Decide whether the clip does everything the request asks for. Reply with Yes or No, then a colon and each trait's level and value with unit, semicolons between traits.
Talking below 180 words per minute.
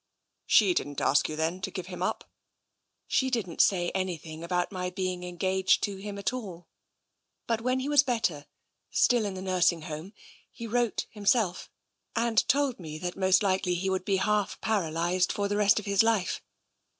No: average, 185 wpm